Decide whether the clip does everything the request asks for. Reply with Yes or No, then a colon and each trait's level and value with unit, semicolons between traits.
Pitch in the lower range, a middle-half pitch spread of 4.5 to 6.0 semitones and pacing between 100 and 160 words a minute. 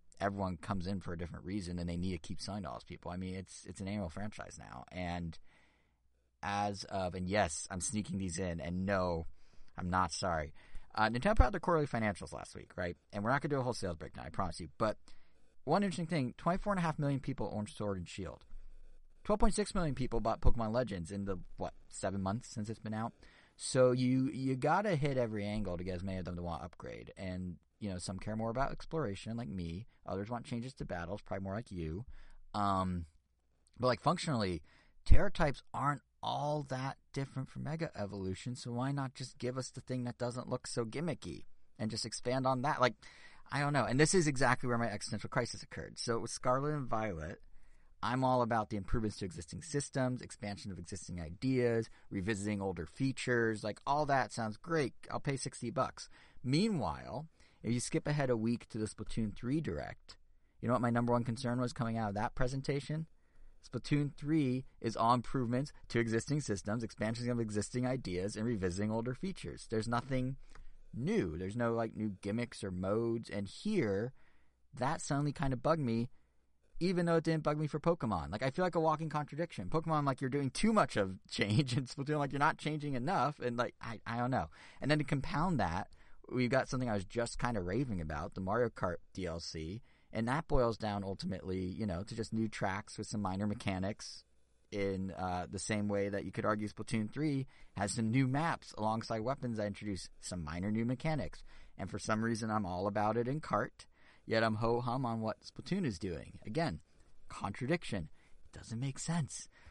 No: low, 115 Hz; wide, 5.4 semitones; fast, 205 wpm